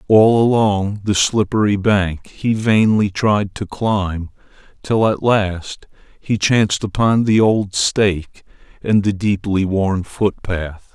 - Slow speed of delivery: Yes, slow, 130 wpm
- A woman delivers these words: No, male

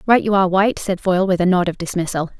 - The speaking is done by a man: No, female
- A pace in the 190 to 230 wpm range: No, fast, 275 wpm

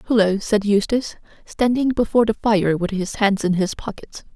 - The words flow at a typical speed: Yes, average, 180 wpm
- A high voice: Yes, high, 210 Hz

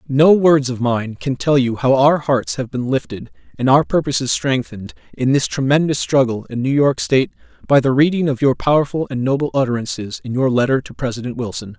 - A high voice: No, low, 135 Hz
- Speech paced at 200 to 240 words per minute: Yes, fast, 205 wpm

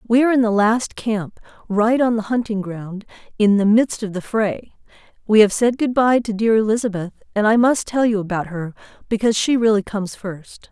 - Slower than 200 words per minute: No, fast, 205 wpm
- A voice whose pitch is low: No, high, 215 Hz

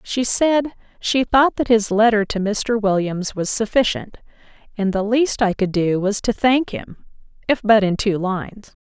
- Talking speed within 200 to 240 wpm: No, average, 185 wpm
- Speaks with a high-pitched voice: Yes, high, 215 Hz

